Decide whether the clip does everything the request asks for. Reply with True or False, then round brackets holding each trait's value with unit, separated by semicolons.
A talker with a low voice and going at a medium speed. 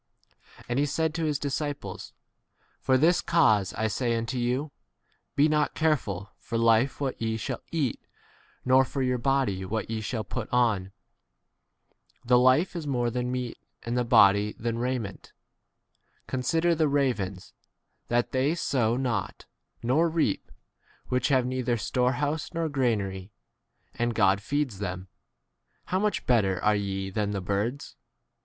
True (125 Hz; 160 wpm)